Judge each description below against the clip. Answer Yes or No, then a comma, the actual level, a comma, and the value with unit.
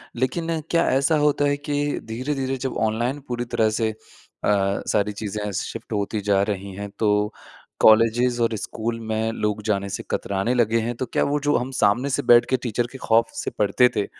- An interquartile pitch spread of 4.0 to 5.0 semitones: No, average, 3.4 semitones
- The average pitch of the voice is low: Yes, low, 115 Hz